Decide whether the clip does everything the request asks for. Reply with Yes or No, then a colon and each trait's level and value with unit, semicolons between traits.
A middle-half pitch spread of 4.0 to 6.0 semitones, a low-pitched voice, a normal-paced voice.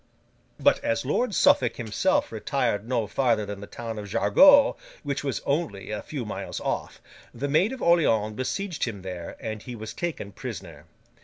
Yes: wide, 5.6 semitones; low, 115 Hz; average, 170 wpm